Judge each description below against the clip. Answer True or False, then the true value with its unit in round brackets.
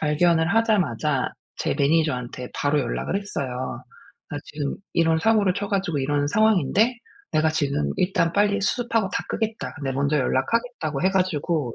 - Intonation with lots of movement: True (6.2 semitones)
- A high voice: False (160 Hz)